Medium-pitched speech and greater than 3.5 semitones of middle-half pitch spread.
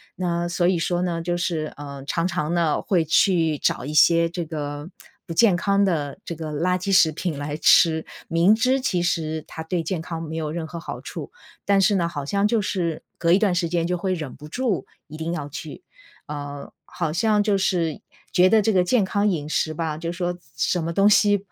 No: medium, 170 Hz; average, 2.9 semitones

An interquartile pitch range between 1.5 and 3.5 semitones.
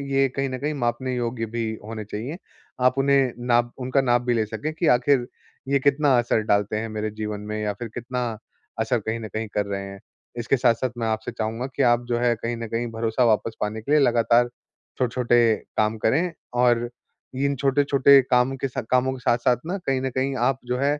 Yes: average, 2.9 semitones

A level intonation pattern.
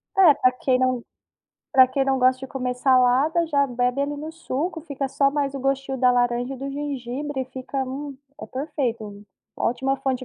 Yes: narrow, 1.9 semitones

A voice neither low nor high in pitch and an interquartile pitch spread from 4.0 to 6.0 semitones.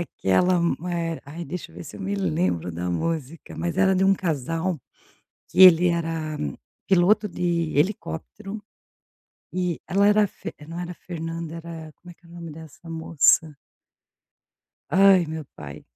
No: medium, 170 Hz; narrow, 2.5 semitones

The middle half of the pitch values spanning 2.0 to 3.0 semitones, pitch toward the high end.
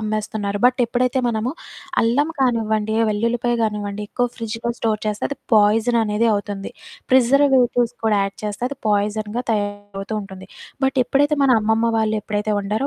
Yes: average, 2.7 semitones; high, 220 Hz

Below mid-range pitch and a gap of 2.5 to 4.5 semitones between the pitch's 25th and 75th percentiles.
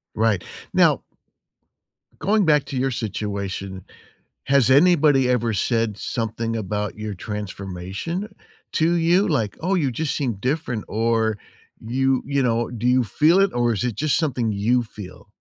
No: low, 120 Hz; average, 5.1 semitones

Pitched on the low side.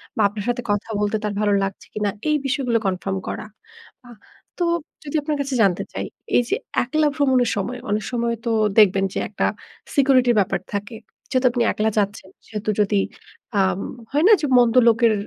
No: high, 225 Hz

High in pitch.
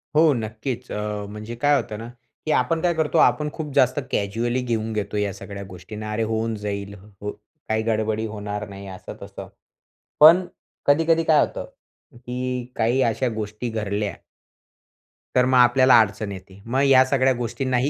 No: low, 115 Hz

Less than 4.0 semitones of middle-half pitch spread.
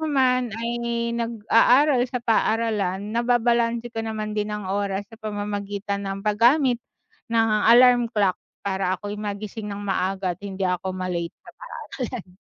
Yes: average, 2.9 semitones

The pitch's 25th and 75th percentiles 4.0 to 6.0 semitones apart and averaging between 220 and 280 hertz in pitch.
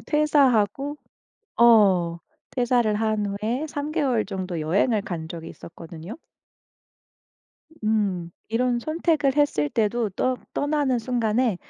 Yes: wide, 5.4 semitones; high, 225 Hz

